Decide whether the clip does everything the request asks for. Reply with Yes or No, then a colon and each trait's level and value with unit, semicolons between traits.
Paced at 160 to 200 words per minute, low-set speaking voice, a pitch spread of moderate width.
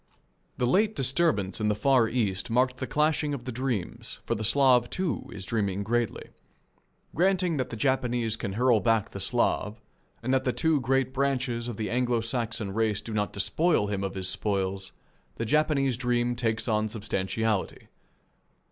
Yes: average, 170 wpm; low, 120 Hz; average, 3.7 semitones